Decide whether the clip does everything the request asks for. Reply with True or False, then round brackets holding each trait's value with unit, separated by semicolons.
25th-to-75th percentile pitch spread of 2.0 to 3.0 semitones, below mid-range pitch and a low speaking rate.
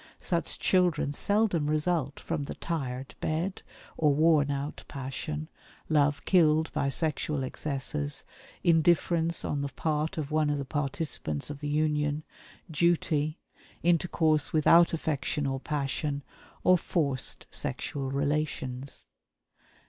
False (2.4 semitones; 150 Hz; 120 wpm)